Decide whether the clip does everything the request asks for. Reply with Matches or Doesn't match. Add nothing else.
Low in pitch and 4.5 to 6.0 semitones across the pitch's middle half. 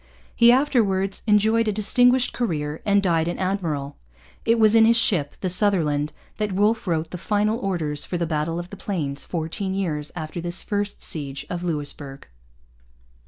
Doesn't match